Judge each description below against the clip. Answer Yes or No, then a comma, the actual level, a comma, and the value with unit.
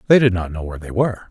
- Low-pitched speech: Yes, low, 100 Hz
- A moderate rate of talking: No, fast, 320 wpm